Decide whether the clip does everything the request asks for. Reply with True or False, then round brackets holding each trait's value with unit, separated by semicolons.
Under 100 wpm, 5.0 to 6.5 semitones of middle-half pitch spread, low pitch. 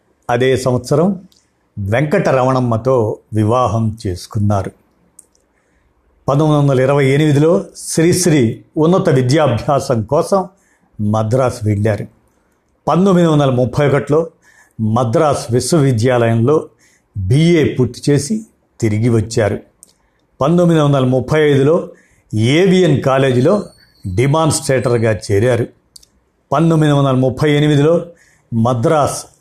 True (80 wpm; 5.3 semitones; 130 Hz)